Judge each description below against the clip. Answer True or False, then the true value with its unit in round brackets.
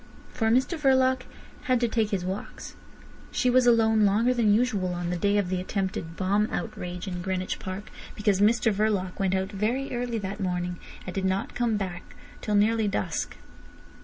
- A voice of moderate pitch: False (205 Hz)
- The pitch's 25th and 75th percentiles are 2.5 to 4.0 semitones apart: True (3.5 semitones)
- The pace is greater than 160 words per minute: True (180 wpm)